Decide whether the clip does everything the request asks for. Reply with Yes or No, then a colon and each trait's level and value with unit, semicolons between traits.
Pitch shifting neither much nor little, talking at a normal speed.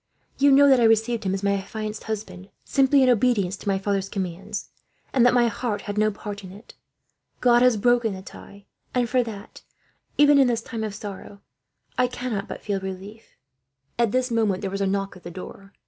No: average, 3.5 semitones; fast, 210 wpm